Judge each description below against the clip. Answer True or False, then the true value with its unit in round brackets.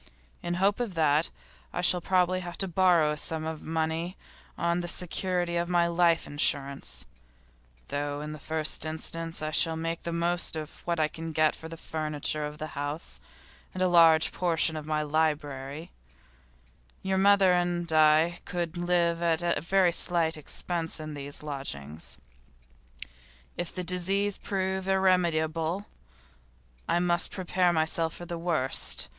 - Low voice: False (165 Hz)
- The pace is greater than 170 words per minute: False (150 wpm)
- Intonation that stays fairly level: True (2.2 semitones)